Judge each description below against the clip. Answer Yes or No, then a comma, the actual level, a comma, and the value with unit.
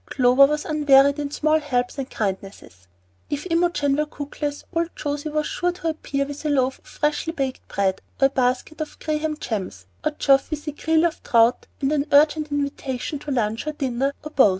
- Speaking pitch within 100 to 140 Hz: No, very high, 285 Hz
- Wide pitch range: No, narrow, 2.6 semitones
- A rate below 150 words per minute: No, average, 195 wpm